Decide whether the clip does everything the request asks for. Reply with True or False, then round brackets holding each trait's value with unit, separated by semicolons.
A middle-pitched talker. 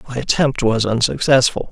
False (125 Hz)